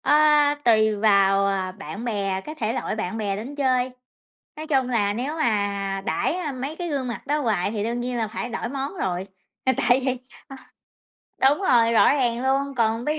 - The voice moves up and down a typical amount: Yes, average, 4.7 semitones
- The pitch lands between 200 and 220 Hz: No, high, 235 Hz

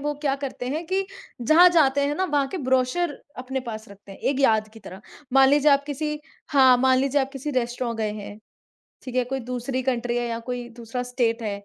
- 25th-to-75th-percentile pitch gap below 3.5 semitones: Yes, average, 3.0 semitones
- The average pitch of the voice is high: Yes, very high, 260 Hz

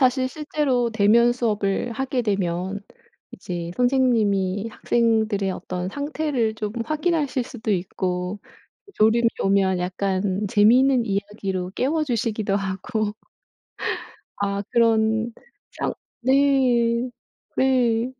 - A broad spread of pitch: No, average, 4.2 semitones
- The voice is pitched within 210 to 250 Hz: Yes, high, 220 Hz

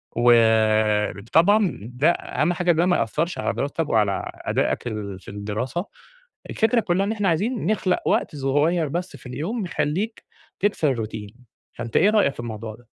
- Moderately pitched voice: Yes, medium, 150 Hz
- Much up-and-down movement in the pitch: Yes, wide, 8.1 semitones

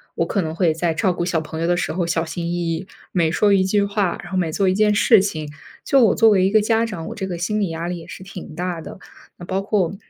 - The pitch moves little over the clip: No, average, 3.3 semitones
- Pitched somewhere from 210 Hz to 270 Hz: No, medium, 185 Hz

